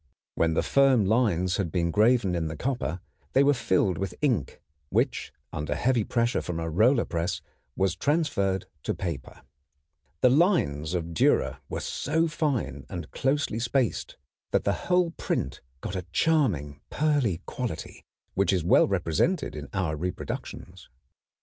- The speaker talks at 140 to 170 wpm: Yes, average, 150 wpm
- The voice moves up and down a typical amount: No, wide, 7.8 semitones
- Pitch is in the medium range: No, very low, 95 Hz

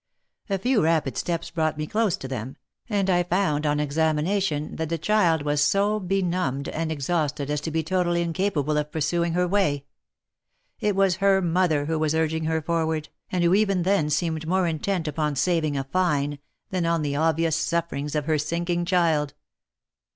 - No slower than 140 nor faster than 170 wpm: No, average, 180 wpm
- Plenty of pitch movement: No, average, 3.1 semitones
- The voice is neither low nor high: Yes, medium, 165 Hz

